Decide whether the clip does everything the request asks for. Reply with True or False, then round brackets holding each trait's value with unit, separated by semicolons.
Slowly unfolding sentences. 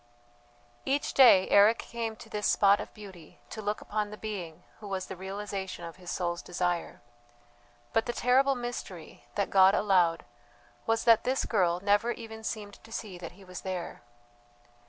False (170 wpm)